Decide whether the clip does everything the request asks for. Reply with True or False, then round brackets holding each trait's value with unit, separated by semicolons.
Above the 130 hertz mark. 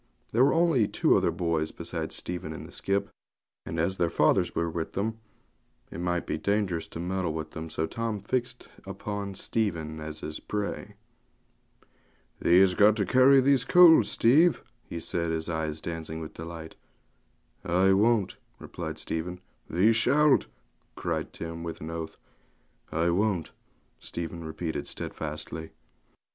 False (90 Hz)